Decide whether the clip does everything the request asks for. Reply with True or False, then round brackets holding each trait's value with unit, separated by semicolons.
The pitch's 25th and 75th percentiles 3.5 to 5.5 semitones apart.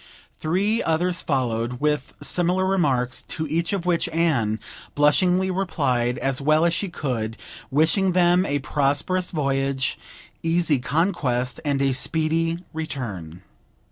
True (4.9 semitones)